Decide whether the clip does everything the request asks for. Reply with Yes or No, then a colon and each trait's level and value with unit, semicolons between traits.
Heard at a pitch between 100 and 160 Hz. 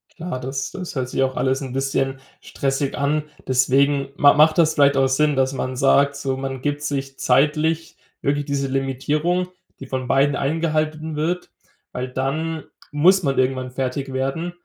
Yes: medium, 140 Hz